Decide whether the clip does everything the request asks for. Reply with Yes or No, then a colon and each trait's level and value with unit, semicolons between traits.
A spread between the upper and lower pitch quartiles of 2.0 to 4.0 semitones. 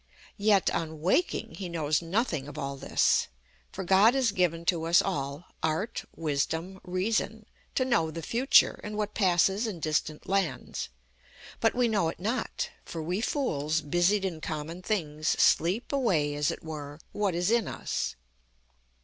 No: average, 5.1 semitones